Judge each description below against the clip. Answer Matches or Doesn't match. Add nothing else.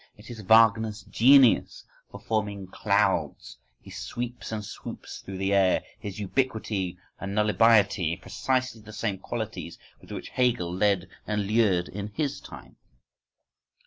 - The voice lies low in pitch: Matches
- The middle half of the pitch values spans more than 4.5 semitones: Doesn't match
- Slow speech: Matches